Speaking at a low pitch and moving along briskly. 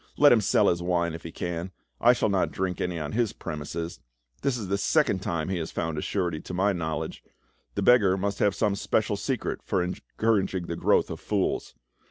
Yes: very low, 95 Hz; fast, 210 wpm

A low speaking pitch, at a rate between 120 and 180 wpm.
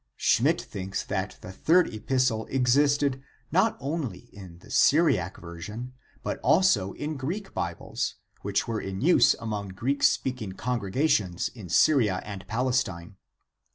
Yes: low, 115 Hz; average, 140 wpm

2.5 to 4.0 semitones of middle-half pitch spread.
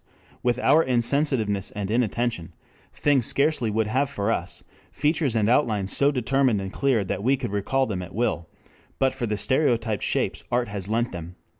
No: average, 4.5 semitones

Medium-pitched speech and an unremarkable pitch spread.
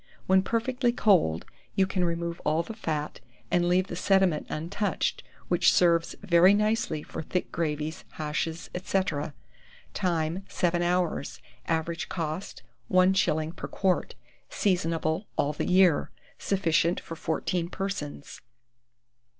Yes: medium, 175 Hz; average, 3.0 semitones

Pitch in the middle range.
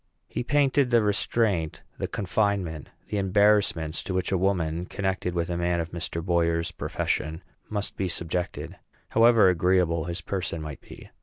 No: very low, 90 Hz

